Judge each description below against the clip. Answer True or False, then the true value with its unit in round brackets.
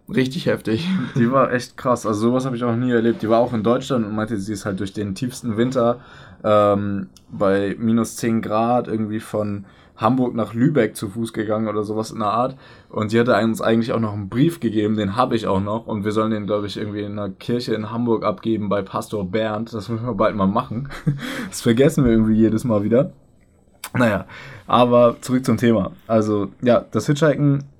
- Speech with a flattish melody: True (2.2 semitones)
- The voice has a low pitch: True (110 Hz)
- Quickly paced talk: True (210 wpm)